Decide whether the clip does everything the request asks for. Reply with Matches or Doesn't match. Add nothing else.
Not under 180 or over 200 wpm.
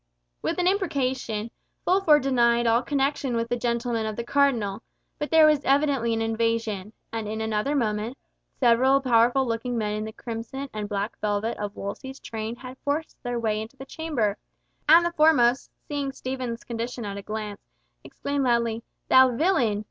Doesn't match